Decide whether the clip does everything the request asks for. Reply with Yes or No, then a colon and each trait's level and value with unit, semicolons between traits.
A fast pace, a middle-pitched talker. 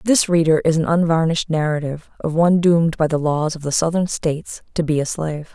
Yes: fast, 215 wpm; medium, 160 Hz